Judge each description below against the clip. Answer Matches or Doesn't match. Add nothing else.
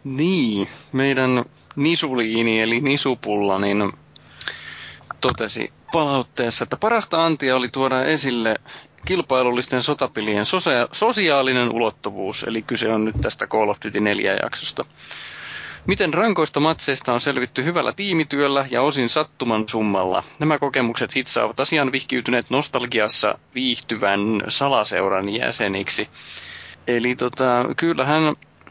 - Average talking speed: Matches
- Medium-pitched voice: Doesn't match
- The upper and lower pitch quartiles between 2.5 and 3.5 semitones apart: Doesn't match